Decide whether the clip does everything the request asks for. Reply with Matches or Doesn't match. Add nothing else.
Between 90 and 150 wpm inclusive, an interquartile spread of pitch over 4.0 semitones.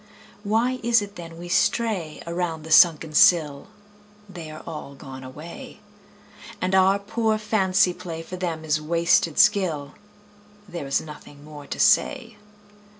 Matches